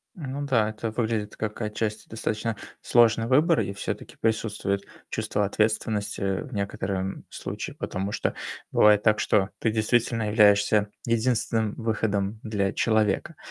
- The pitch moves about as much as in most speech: No, narrow, 1.8 semitones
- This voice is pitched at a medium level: No, low, 110 Hz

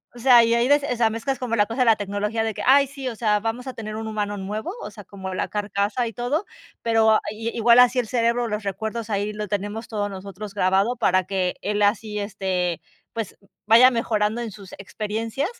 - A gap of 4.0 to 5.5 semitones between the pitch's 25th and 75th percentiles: No, narrow, 2.4 semitones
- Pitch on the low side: No, high, 220 Hz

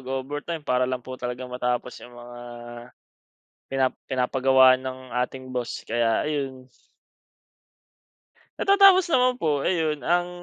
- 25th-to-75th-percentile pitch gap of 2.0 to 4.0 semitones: Yes, average, 3.2 semitones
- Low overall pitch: Yes, low, 130 Hz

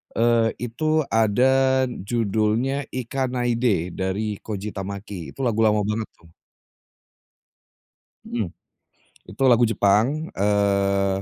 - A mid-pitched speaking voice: No, low, 110 Hz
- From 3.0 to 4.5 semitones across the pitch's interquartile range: Yes, average, 3.6 semitones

